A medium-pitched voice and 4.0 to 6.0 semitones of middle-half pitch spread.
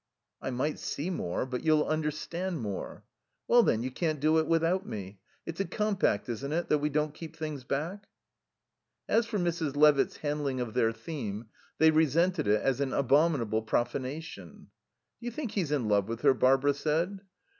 Yes: medium, 150 Hz; average, 4.6 semitones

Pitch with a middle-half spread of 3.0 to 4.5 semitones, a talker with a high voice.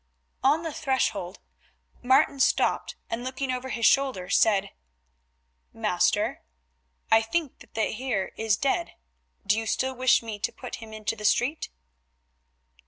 Yes: average, 3.6 semitones; high, 245 Hz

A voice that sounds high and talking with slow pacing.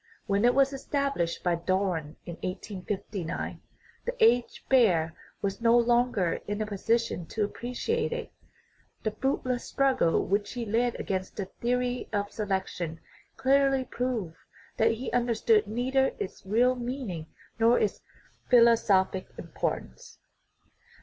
Yes: high, 225 Hz; slow, 130 wpm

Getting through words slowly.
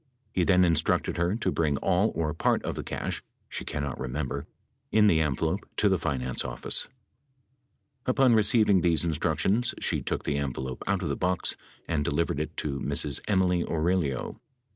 No: average, 165 wpm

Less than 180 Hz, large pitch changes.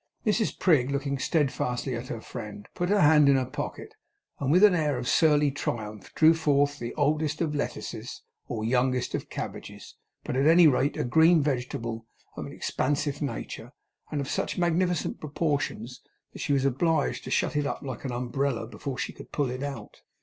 No: medium, 140 Hz; average, 3.5 semitones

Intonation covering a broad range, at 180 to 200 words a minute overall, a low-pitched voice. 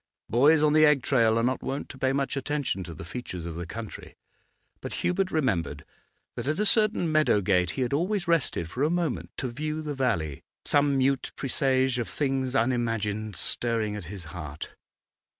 Yes: wide, 6.0 semitones; average, 185 wpm; low, 130 Hz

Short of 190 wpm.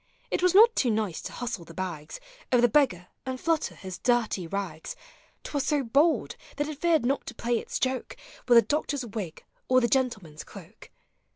No: average, 195 wpm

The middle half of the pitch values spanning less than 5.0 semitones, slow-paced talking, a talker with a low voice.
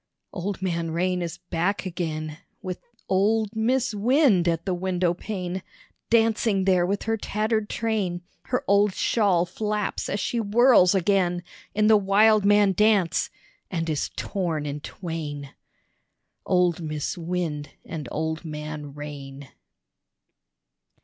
No: average, 4.1 semitones; slow, 125 wpm; medium, 185 Hz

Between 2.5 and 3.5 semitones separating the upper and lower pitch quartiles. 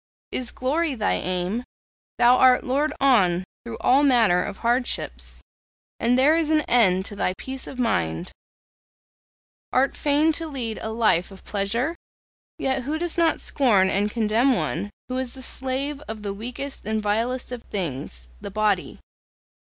No: average, 4.7 semitones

